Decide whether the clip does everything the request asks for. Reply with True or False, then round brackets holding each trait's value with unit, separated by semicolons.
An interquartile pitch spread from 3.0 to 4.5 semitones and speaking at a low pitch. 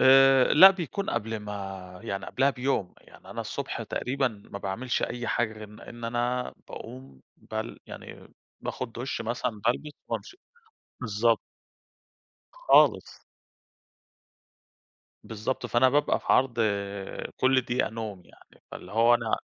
True (3.6 semitones; 120 Hz)